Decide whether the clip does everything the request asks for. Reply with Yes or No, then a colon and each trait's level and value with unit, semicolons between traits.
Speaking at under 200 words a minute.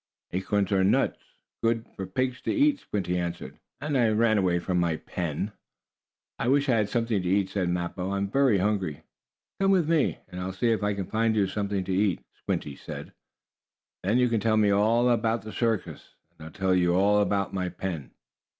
No: fast, 205 wpm